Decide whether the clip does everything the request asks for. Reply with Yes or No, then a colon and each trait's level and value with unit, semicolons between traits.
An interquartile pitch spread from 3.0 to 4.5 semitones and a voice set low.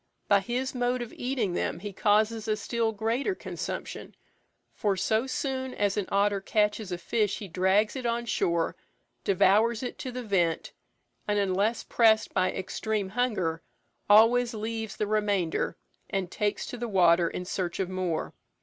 No: average, 3.6 semitones; high, 210 Hz